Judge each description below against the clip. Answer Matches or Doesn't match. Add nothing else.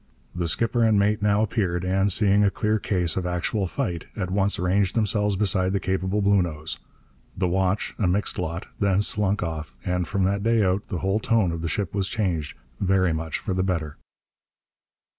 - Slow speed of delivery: Doesn't match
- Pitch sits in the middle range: Doesn't match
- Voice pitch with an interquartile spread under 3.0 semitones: Matches